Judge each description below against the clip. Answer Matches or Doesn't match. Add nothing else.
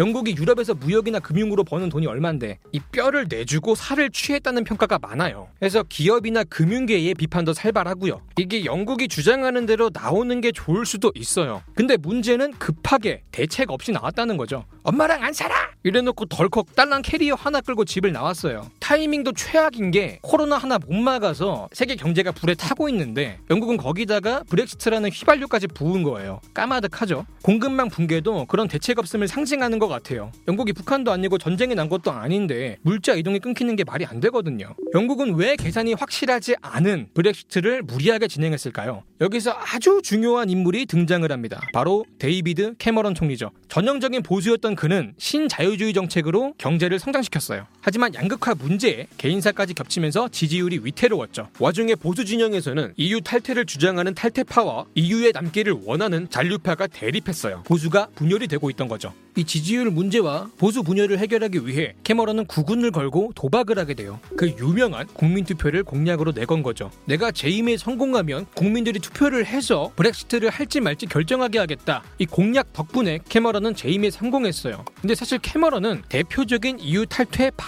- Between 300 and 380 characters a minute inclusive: Doesn't match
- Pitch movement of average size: Doesn't match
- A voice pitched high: Matches